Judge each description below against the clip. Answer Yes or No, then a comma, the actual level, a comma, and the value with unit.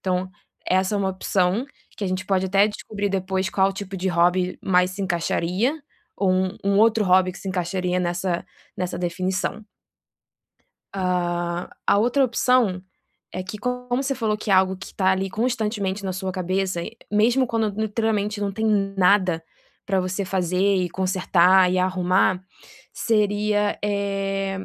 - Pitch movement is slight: Yes, narrow, 2.1 semitones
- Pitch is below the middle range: No, high, 190 Hz